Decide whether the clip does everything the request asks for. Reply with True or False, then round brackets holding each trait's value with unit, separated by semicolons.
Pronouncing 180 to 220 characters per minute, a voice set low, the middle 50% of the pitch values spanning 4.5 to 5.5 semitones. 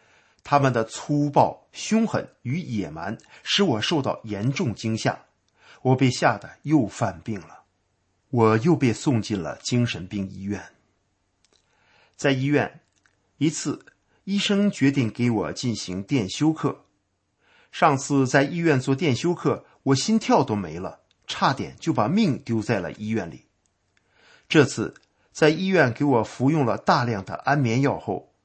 True (205 characters per minute; 130 Hz; 4.9 semitones)